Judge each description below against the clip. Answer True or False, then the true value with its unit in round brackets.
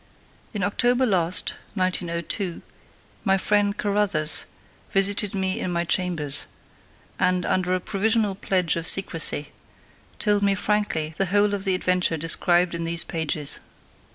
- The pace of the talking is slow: True (130 wpm)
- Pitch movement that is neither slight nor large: True (3.2 semitones)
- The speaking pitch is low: False (185 Hz)